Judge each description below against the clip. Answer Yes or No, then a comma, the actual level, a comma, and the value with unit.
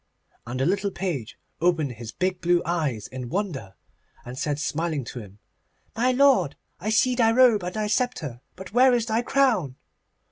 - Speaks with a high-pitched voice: No, medium, 180 Hz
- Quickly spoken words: No, average, 175 wpm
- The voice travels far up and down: Yes, wide, 9.0 semitones